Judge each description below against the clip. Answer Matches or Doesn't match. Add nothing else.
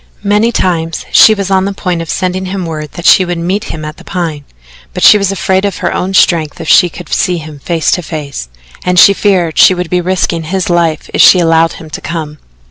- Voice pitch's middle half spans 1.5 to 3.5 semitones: Matches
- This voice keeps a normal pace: Doesn't match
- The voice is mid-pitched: Matches